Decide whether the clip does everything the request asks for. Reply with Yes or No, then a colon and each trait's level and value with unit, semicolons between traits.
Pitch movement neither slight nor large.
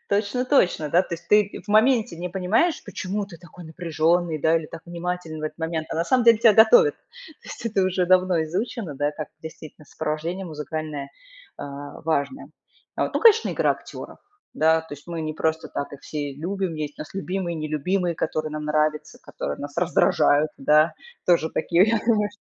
Yes: average, 4.0 semitones